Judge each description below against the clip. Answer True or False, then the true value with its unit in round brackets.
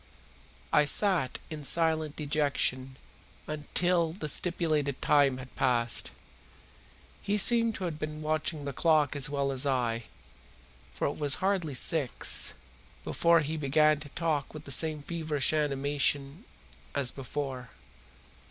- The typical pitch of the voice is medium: True (150 Hz)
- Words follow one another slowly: True (130 wpm)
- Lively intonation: False (2.6 semitones)